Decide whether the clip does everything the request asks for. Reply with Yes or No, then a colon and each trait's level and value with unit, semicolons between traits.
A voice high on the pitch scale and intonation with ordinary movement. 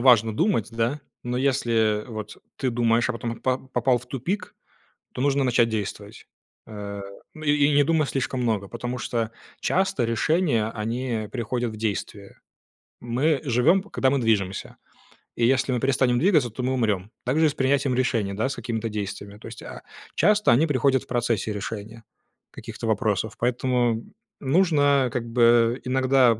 No: low, 120 Hz; average, 3.1 semitones